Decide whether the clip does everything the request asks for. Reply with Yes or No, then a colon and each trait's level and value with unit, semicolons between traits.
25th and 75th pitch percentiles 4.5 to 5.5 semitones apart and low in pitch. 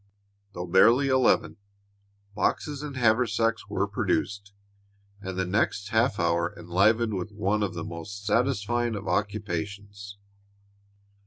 No: average, 3.2 semitones; low, 100 Hz